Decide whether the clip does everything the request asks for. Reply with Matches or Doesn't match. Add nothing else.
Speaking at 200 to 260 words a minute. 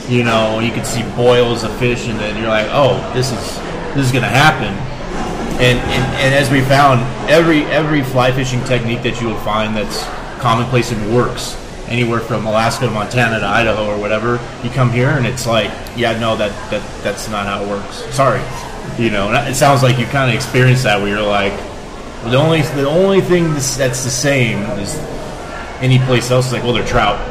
Matches